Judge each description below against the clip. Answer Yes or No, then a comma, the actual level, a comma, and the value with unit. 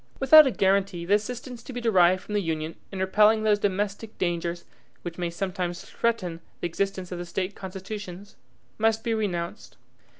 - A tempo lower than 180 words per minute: Yes, average, 170 wpm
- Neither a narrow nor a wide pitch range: Yes, average, 3.5 semitones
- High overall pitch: Yes, high, 195 Hz